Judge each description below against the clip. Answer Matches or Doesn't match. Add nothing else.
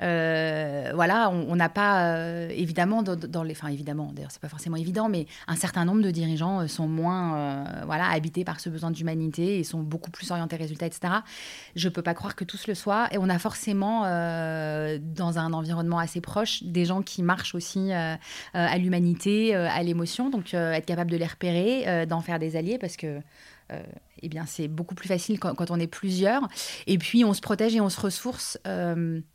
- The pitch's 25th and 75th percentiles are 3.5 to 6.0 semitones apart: Doesn't match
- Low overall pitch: Doesn't match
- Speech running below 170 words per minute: Doesn't match